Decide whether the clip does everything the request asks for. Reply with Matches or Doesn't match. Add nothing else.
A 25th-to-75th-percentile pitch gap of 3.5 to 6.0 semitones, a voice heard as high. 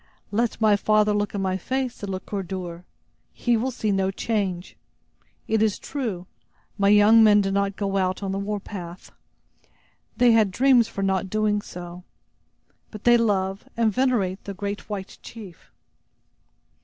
Doesn't match